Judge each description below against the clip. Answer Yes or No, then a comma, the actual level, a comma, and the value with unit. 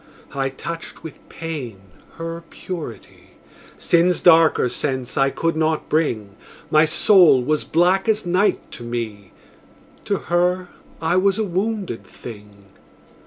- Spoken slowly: Yes, slow, 125 wpm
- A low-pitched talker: No, medium, 160 Hz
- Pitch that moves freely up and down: Yes, wide, 5.7 semitones